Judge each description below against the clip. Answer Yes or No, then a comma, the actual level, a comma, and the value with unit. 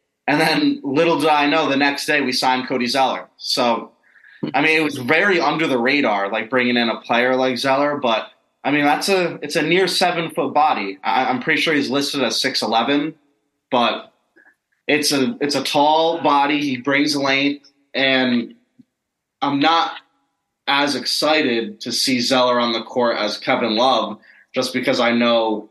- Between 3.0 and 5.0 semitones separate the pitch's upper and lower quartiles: Yes, average, 3.4 semitones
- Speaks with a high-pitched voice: No, medium, 140 Hz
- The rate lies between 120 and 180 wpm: Yes, average, 175 wpm